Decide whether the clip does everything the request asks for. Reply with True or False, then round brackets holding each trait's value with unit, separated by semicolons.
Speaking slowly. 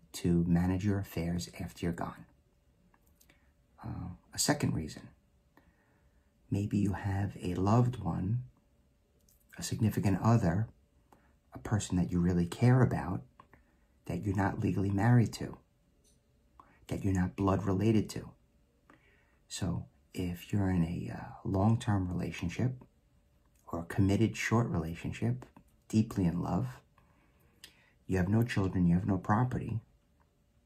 True (125 wpm)